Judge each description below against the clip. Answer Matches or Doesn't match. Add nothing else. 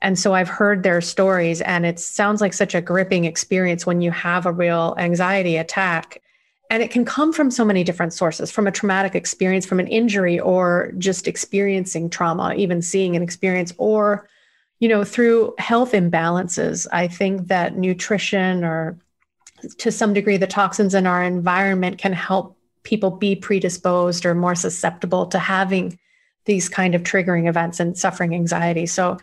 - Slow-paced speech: Doesn't match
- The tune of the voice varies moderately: Doesn't match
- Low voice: Doesn't match